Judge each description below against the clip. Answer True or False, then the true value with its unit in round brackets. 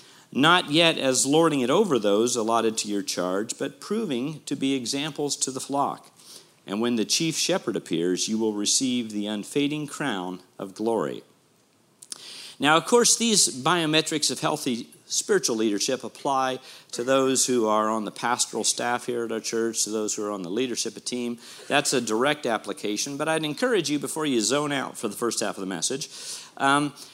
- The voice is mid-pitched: False (130 Hz)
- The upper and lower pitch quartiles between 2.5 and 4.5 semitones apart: False (5.0 semitones)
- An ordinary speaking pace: True (185 wpm)